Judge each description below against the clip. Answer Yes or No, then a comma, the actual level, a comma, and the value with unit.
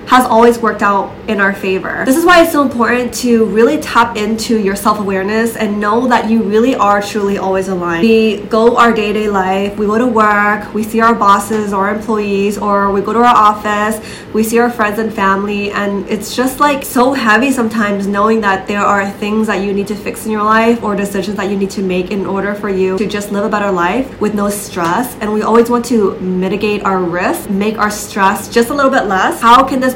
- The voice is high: Yes, high, 210 Hz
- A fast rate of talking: Yes, fast, 235 wpm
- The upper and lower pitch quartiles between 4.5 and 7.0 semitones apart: No, narrow, 2.4 semitones